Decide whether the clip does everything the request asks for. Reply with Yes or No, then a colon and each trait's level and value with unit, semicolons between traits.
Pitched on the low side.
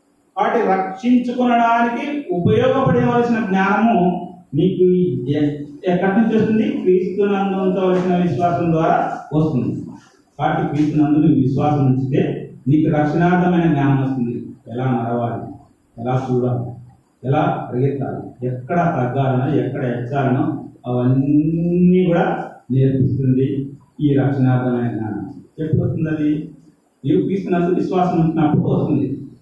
No: medium, 150 Hz